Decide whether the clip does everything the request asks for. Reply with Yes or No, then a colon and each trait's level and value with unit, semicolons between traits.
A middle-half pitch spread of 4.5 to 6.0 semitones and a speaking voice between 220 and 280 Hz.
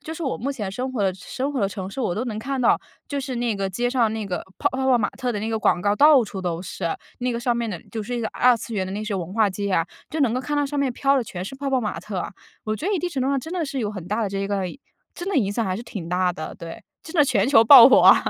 Yes: average, 5.2 semitones; high, 230 Hz